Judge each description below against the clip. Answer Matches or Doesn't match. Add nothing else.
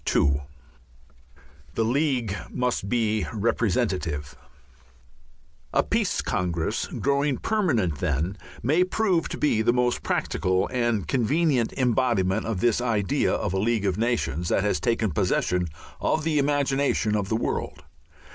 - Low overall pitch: Matches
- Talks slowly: Matches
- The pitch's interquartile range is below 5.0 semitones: Doesn't match